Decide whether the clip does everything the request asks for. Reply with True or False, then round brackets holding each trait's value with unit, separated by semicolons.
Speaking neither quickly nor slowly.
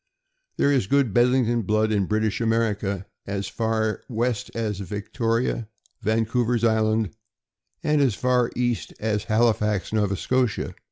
False (125 wpm)